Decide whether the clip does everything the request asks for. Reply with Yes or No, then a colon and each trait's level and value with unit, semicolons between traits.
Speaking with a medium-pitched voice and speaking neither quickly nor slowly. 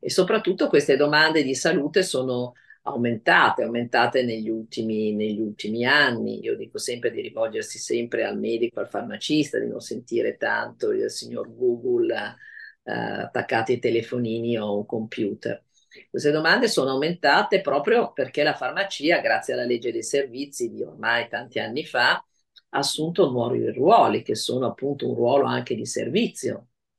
Yes: medium, 150 Hz; average, 155 wpm